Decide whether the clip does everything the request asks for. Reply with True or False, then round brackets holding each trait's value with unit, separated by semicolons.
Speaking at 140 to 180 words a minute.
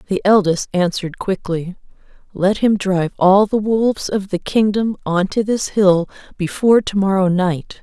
True (160 wpm)